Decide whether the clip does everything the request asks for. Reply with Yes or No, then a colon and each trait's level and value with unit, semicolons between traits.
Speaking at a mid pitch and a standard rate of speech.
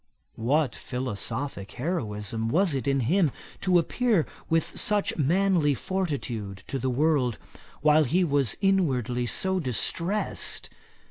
No: medium, 145 Hz; slow, 120 wpm